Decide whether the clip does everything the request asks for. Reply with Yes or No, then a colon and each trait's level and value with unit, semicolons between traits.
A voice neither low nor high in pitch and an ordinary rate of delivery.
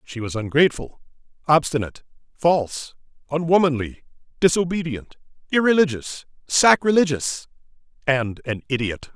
No: medium, 145 Hz; slow, 80 wpm